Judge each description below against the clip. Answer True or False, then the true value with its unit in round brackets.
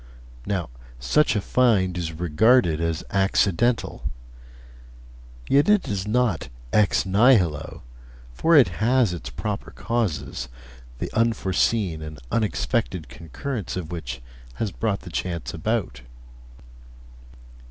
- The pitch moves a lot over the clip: True (5.9 semitones)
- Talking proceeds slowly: True (110 wpm)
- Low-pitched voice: True (95 Hz)